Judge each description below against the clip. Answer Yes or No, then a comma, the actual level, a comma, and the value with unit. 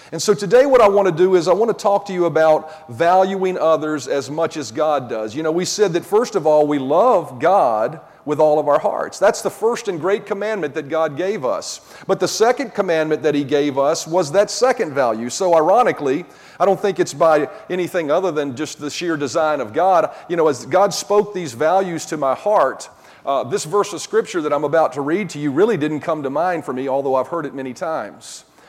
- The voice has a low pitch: No, medium, 165 Hz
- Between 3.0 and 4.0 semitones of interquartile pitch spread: No, average, 4.9 semitones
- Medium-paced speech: No, fast, 235 wpm